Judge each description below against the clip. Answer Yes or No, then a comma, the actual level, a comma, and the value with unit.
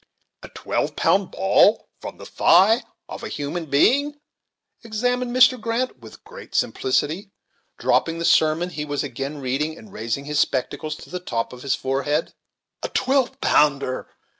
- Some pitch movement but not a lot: No, wide, 8.3 semitones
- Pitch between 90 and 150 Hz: No, medium, 165 Hz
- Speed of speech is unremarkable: Yes, average, 155 wpm